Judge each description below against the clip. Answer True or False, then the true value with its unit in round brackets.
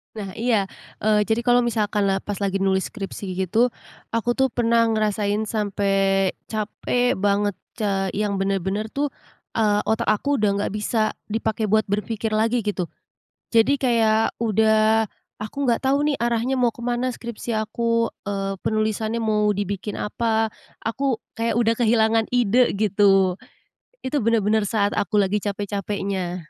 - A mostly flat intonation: True (2.3 semitones)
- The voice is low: False (215 Hz)